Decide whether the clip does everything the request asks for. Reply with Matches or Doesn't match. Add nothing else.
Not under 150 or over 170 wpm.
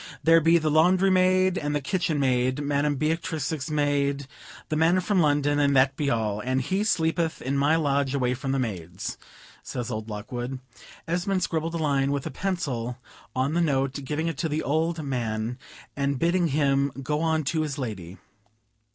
Doesn't match